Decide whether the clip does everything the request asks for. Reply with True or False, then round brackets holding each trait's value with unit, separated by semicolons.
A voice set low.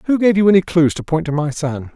False (165 Hz)